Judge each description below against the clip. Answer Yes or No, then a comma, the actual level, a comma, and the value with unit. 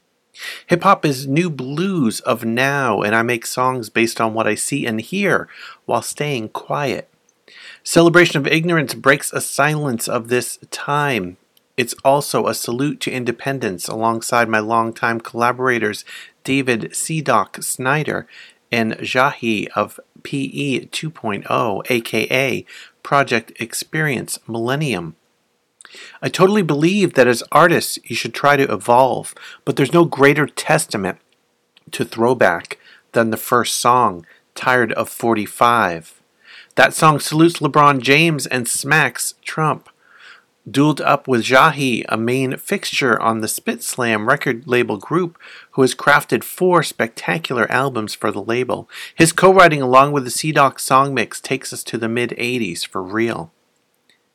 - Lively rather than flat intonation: No, average, 4.4 semitones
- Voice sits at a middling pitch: No, low, 130 Hz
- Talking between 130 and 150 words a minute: Yes, average, 140 wpm